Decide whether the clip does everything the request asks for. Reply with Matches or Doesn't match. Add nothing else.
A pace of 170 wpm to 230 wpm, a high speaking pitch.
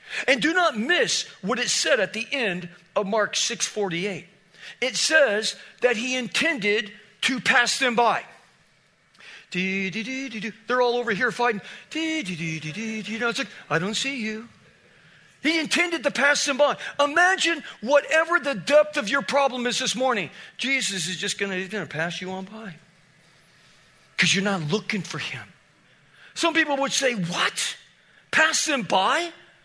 Doesn't match